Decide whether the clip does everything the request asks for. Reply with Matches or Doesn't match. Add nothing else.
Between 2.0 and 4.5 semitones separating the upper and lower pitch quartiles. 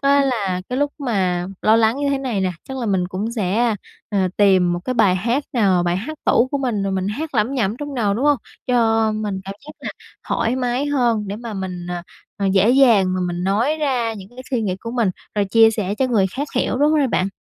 Doesn't match